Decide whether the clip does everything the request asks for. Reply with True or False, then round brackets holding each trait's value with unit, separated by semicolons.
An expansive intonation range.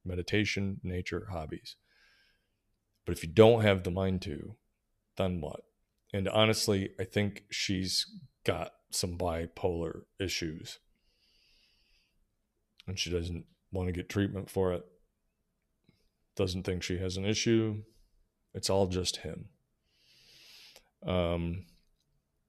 False (2.8 semitones)